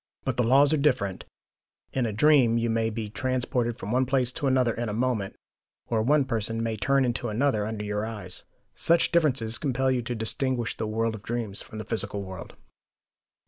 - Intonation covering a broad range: No, average, 3.1 semitones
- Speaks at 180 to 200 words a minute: Yes, average, 195 wpm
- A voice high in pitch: No, low, 115 Hz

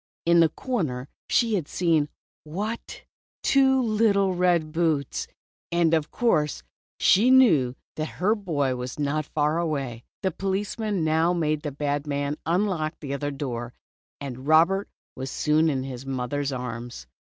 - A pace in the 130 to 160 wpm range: Yes, average, 155 wpm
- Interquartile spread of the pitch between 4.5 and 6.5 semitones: Yes, average, 4.8 semitones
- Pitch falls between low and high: Yes, medium, 155 Hz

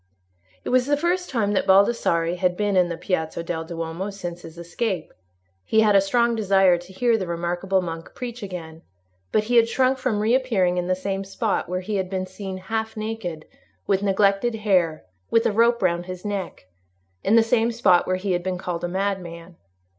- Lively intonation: No, average, 4.0 semitones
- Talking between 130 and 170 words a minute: No, average, 195 wpm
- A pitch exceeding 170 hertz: Yes, high, 190 Hz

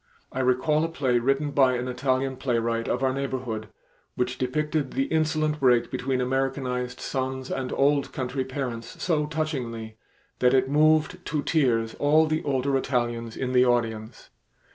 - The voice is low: Yes, low, 130 Hz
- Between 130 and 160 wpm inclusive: Yes, average, 155 wpm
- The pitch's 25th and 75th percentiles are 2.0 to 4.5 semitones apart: Yes, average, 2.8 semitones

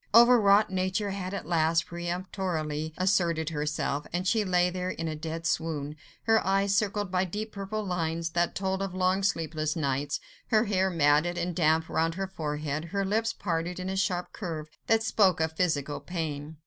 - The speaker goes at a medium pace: Yes, average, 175 wpm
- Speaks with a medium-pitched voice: Yes, medium, 175 Hz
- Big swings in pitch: No, average, 3.3 semitones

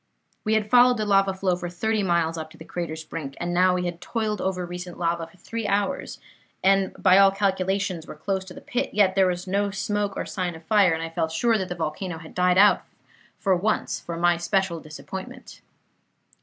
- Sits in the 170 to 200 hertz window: Yes, medium, 185 Hz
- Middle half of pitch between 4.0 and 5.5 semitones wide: No, average, 2.8 semitones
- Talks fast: Yes, fast, 215 wpm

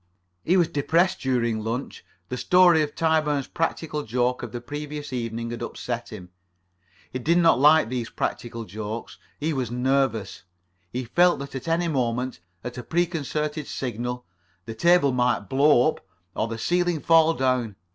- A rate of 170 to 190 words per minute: No, average, 160 wpm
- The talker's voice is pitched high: No, low, 130 Hz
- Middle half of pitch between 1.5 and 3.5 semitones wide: No, average, 4.8 semitones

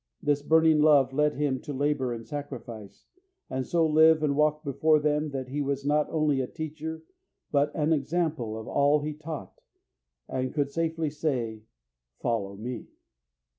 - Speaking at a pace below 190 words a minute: Yes, average, 160 wpm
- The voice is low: No, medium, 145 Hz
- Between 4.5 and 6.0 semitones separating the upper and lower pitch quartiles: No, average, 2.9 semitones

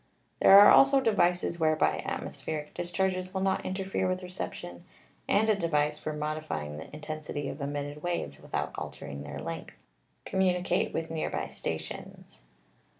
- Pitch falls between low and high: Yes, medium, 165 Hz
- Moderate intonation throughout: Yes, average, 4.1 semitones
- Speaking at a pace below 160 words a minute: Yes, average, 150 wpm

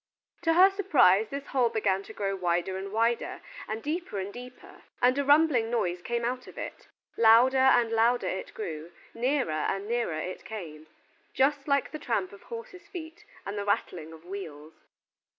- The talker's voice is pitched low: No, high, 230 Hz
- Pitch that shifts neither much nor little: No, wide, 6.3 semitones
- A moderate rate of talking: Yes, average, 175 wpm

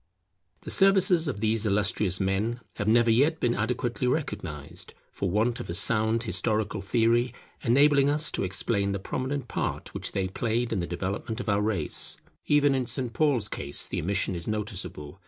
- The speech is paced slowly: No, average, 175 wpm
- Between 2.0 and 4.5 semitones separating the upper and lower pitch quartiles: Yes, average, 4.2 semitones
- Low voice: Yes, low, 110 Hz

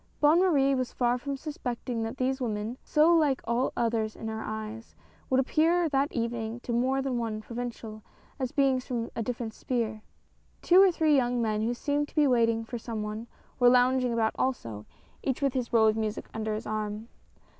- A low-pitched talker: No, high, 240 Hz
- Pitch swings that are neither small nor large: Yes, average, 3.3 semitones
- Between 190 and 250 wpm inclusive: Yes, average, 195 wpm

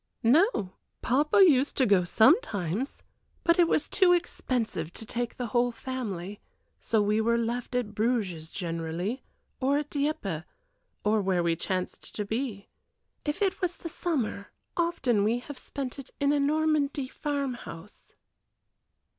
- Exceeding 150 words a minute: No, average, 145 wpm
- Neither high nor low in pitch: No, high, 245 Hz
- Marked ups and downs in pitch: Yes, wide, 6.1 semitones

